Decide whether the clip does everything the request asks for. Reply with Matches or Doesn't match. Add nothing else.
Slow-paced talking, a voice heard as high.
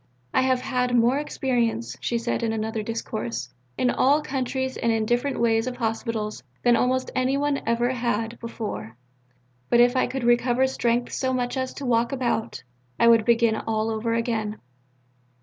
Doesn't match